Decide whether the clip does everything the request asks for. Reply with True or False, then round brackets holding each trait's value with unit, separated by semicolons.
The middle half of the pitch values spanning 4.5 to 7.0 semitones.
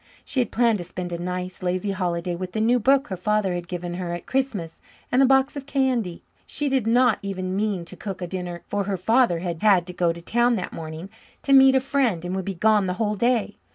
True (5.2 semitones)